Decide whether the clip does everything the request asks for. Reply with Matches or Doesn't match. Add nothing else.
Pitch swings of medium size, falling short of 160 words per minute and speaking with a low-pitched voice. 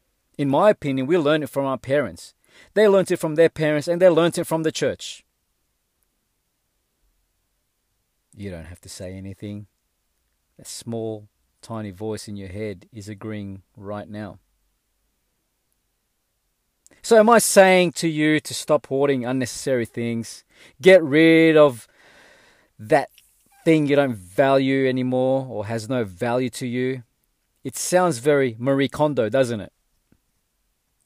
Doesn't match